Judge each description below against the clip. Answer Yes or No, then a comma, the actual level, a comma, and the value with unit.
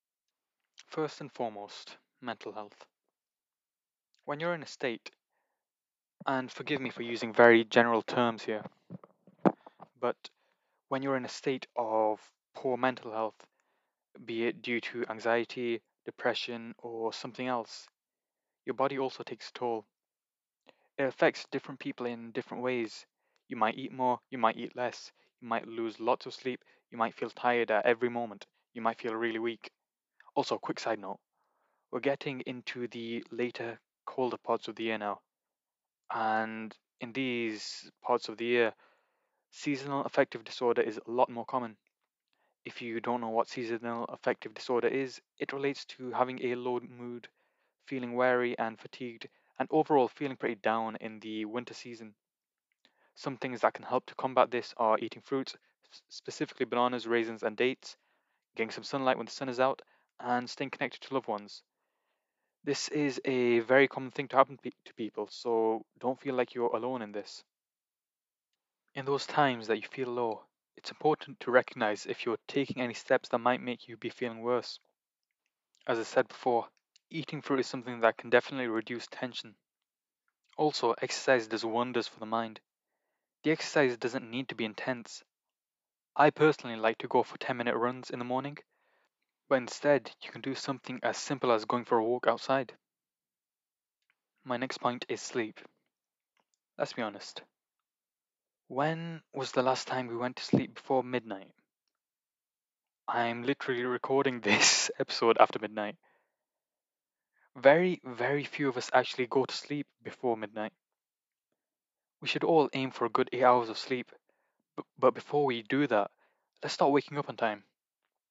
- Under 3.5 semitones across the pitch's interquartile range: Yes, narrow, 2.4 semitones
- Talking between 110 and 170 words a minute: Yes, average, 160 wpm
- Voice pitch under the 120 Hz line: No, low, 125 Hz